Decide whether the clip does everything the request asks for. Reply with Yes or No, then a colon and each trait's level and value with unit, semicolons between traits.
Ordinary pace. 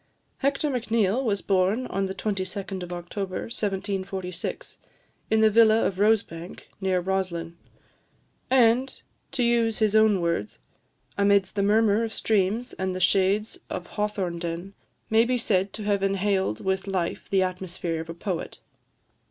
Yes: average, 145 wpm